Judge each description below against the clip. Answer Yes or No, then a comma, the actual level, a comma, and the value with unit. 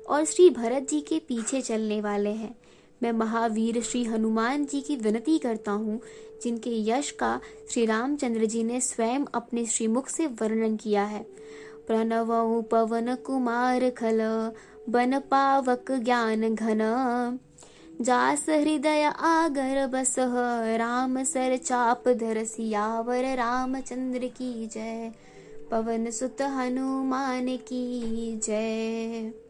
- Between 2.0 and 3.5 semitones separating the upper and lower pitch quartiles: Yes, average, 2.8 semitones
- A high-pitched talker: Yes, high, 245 Hz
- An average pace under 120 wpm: Yes, slow, 110 wpm